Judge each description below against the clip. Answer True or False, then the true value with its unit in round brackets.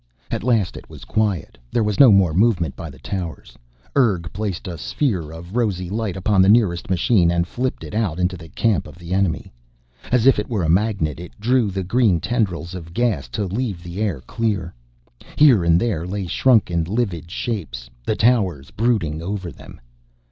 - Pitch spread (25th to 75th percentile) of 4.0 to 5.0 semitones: True (4.5 semitones)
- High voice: False (95 Hz)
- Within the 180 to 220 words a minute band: True (190 wpm)